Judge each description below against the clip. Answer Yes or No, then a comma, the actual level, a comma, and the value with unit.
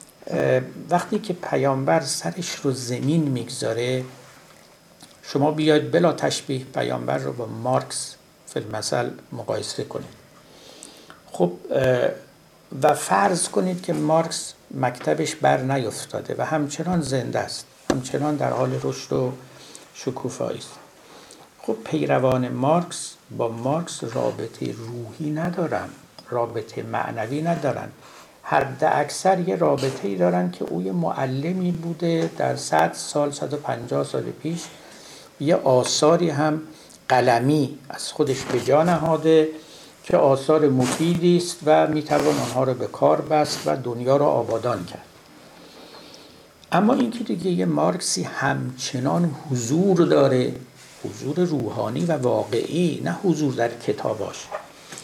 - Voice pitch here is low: No, medium, 150 Hz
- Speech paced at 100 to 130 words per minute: Yes, average, 120 wpm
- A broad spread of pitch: No, average, 4.5 semitones